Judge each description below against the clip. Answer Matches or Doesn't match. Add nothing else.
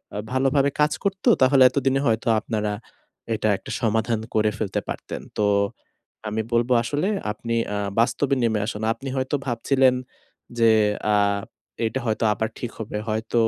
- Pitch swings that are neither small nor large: Matches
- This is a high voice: Doesn't match